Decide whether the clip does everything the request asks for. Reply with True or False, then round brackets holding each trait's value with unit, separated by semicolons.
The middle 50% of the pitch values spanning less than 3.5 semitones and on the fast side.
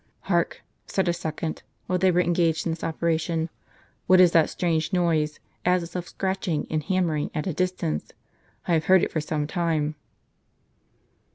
False (2.4 semitones; 180 wpm)